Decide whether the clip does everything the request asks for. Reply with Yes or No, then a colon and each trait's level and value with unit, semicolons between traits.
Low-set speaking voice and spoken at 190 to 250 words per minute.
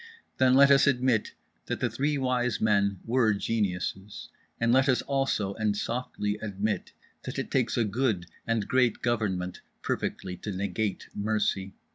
No: low, 110 Hz; average, 150 wpm